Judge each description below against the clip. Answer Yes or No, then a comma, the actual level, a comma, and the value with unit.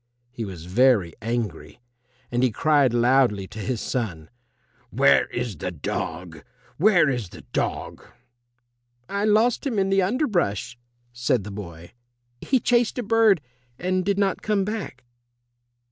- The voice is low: Yes, low, 125 Hz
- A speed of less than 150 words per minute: Yes, average, 140 wpm